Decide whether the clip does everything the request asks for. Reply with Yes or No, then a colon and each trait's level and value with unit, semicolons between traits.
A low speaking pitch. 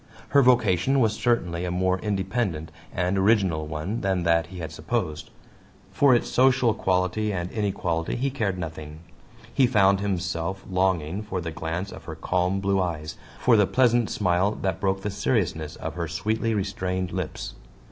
Yes: very low, 95 Hz